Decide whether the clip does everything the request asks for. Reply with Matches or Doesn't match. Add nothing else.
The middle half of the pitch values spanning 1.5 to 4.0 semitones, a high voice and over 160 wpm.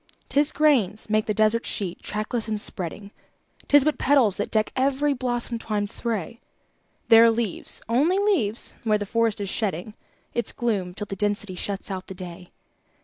Matches